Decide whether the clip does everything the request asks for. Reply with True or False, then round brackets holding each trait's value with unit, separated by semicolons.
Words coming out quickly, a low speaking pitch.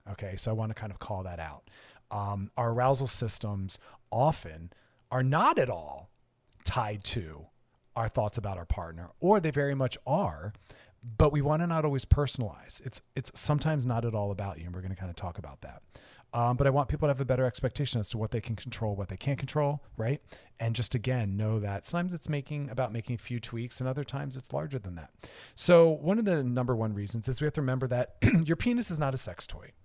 True (235 wpm; 120 Hz)